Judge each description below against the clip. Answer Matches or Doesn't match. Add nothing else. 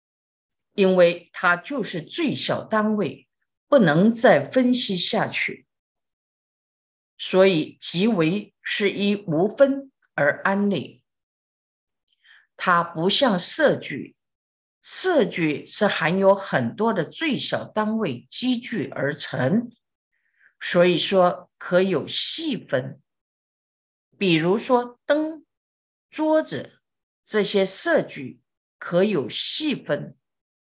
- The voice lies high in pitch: Matches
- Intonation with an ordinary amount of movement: Doesn't match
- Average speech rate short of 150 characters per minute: Matches